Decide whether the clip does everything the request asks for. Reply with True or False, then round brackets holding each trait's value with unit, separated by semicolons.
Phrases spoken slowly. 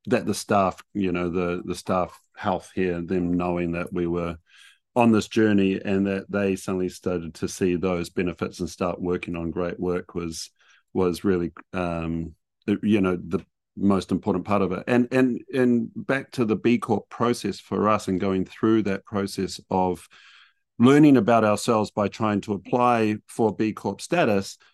False (175 wpm)